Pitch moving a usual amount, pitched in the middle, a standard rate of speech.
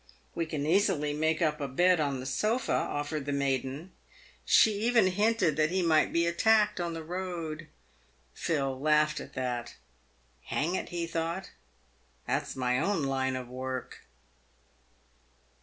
Yes: average, 4.6 semitones; medium, 155 Hz; average, 155 wpm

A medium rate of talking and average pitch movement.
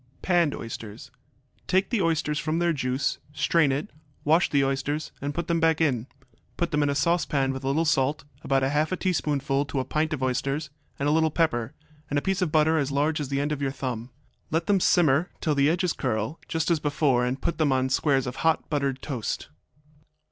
No: fast, 215 wpm; average, 3.1 semitones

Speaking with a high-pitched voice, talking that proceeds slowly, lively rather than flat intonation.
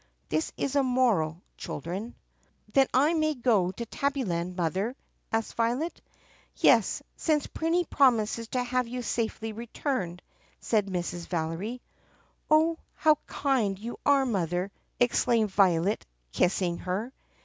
Yes: high, 230 Hz; slow, 125 wpm; wide, 6.3 semitones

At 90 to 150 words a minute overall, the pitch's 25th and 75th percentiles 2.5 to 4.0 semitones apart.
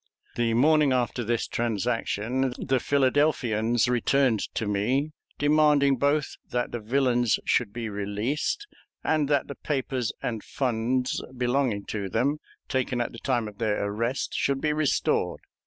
Yes: average, 140 wpm; average, 3.6 semitones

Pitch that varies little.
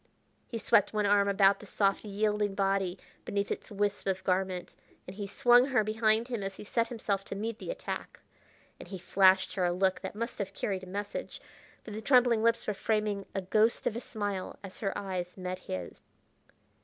Yes: narrow, 2.2 semitones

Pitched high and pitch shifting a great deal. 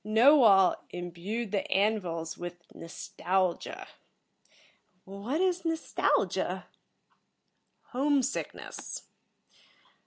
Yes: high, 205 Hz; wide, 7.0 semitones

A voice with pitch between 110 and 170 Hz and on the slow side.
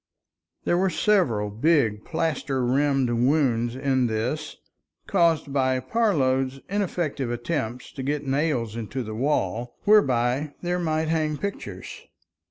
Yes: low, 135 Hz; slow, 120 wpm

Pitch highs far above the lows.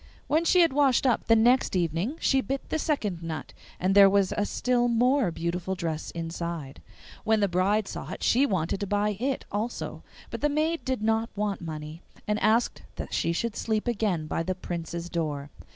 Yes: wide, 6.1 semitones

